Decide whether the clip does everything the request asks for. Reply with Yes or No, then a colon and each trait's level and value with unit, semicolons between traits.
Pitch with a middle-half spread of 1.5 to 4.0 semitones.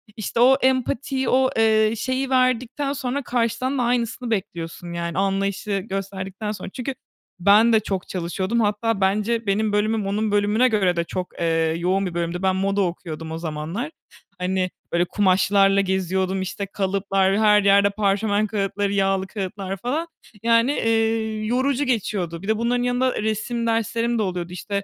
Yes: average, 3.5 semitones